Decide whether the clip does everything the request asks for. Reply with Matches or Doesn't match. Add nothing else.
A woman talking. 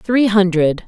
Matches